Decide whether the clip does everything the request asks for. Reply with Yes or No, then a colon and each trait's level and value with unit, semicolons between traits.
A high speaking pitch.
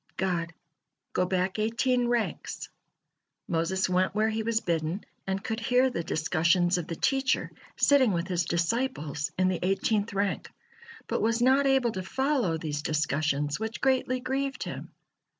Yes: high, 195 Hz